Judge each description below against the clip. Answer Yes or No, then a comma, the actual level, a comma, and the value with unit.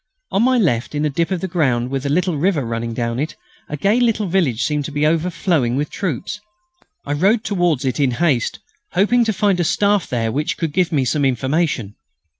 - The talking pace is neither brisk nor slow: No, fast, 210 wpm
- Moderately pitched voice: Yes, medium, 155 Hz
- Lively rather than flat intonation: Yes, wide, 6.0 semitones